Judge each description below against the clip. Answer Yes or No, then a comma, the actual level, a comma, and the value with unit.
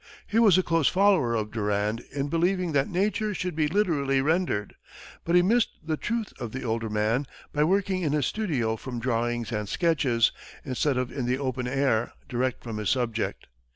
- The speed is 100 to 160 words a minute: No, average, 190 wpm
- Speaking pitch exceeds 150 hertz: No, low, 135 Hz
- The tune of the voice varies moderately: No, wide, 7.1 semitones